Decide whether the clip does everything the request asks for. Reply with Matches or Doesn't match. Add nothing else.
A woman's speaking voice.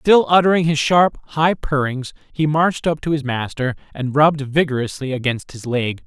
Doesn't match